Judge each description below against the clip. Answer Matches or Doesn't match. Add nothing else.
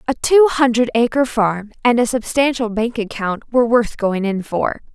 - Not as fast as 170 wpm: Doesn't match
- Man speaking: Doesn't match